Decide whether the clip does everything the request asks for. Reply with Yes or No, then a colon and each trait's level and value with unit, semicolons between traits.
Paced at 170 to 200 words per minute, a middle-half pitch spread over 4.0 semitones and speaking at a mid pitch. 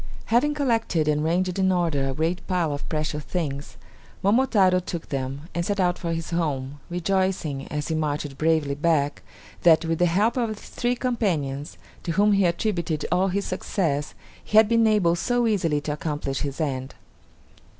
Yes: average, 175 wpm; average, 4.8 semitones; medium, 170 Hz